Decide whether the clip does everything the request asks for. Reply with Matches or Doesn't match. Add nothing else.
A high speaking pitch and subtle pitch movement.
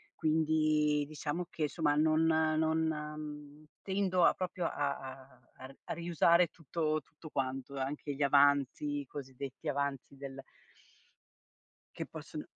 Doesn't match